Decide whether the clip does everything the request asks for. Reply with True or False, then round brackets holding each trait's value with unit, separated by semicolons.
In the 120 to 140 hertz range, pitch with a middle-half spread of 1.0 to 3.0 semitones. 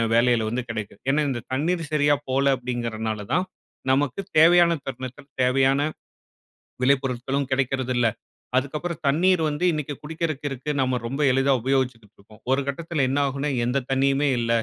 True (135 Hz; 2.7 semitones)